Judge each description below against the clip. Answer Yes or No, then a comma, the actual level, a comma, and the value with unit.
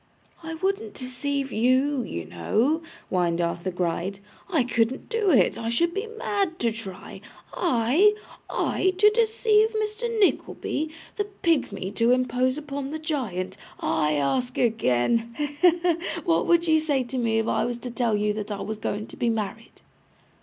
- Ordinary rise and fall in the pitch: No, wide, 7.6 semitones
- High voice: Yes, very high, 255 Hz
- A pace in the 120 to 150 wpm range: No, average, 165 wpm